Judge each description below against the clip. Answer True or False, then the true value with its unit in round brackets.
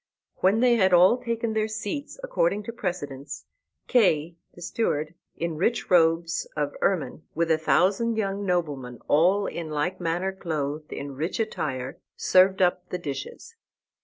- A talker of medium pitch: True (180 Hz)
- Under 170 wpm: True (150 wpm)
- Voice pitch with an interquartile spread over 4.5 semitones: True (5.3 semitones)